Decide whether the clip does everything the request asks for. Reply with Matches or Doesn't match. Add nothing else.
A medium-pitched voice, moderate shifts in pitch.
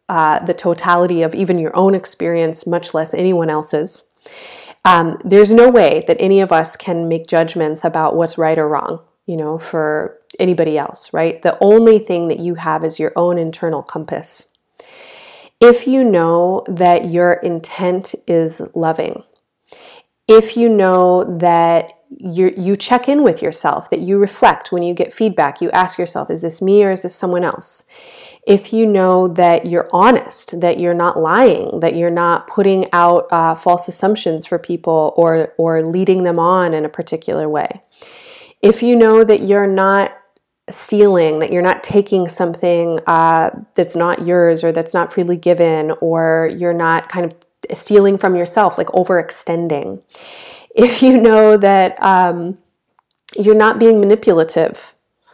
Matches